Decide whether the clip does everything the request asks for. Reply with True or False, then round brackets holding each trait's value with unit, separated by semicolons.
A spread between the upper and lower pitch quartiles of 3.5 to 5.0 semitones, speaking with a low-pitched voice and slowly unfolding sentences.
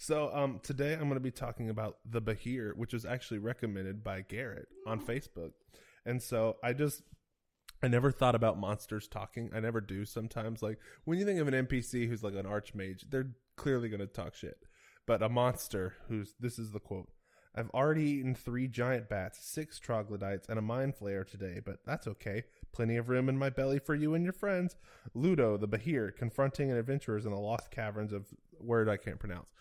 False (3.8 semitones; 115 Hz; 205 wpm)